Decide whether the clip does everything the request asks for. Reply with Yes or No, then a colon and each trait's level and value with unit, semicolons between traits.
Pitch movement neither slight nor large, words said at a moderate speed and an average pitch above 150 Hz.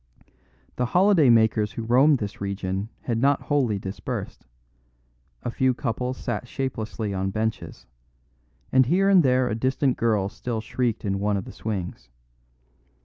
No: average, 4.0 semitones; average, 145 wpm; low, 115 Hz